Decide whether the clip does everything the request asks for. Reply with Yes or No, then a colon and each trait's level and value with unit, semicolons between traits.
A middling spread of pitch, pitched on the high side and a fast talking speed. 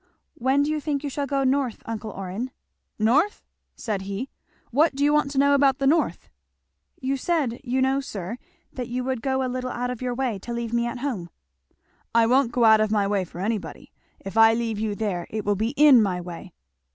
Yes: average, 3.9 semitones; high, 245 Hz; fast, 220 wpm